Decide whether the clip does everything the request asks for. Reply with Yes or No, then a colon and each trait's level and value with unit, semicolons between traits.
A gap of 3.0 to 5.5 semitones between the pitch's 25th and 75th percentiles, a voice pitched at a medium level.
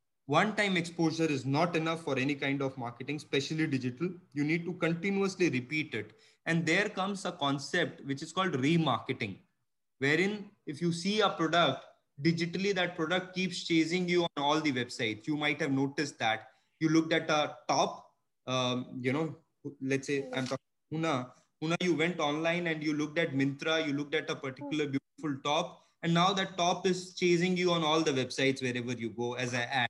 Yes: average, 3.9 semitones; medium, 155 Hz